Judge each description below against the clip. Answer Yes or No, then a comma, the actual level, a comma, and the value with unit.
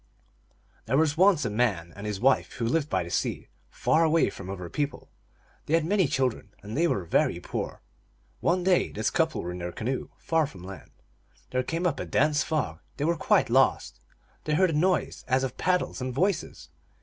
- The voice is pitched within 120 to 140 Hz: Yes, low, 135 Hz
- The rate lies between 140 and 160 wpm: No, average, 200 wpm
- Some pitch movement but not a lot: No, wide, 7.7 semitones